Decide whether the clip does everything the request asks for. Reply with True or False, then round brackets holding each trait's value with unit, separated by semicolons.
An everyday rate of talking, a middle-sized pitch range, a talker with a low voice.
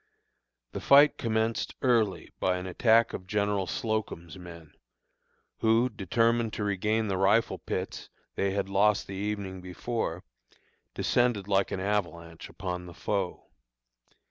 False (130 wpm; 3.2 semitones; 100 Hz)